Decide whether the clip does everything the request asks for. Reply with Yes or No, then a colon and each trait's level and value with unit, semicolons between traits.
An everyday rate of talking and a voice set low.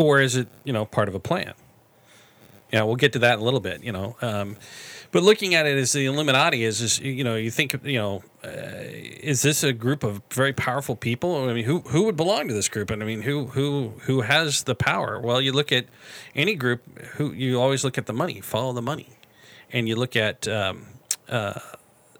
No: fast, 230 wpm; low, 130 Hz